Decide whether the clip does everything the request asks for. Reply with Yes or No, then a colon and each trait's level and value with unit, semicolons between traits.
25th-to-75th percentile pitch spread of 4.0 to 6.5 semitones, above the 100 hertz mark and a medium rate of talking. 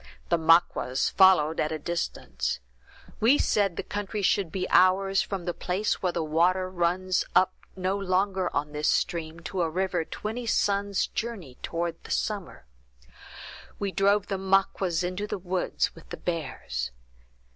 No: average, 2.7 semitones; medium, 185 Hz; average, 155 wpm